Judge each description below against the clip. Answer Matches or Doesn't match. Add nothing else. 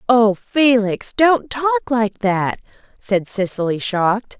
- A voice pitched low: Doesn't match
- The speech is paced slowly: Matches